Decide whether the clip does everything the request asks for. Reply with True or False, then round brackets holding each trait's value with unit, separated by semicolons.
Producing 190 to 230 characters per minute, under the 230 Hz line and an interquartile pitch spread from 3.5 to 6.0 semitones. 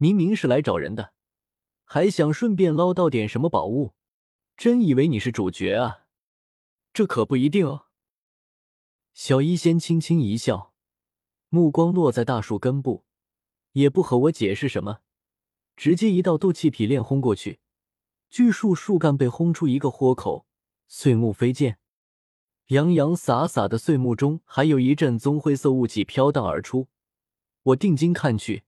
True (225 characters per minute; 140 Hz; 5.7 semitones)